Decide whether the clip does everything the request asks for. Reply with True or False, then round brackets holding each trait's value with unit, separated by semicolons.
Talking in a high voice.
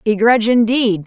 True (225 Hz)